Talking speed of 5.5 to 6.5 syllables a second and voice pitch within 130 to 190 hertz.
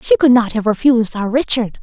No: 5.6 syllables/s; high, 240 Hz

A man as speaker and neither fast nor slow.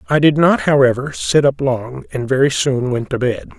No: male; fast, 220 wpm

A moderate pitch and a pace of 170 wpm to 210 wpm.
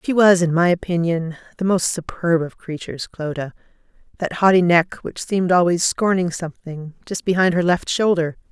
No: medium, 175 Hz; average, 160 wpm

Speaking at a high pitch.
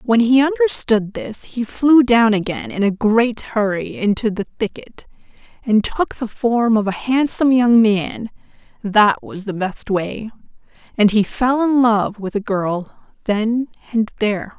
Yes: high, 220 Hz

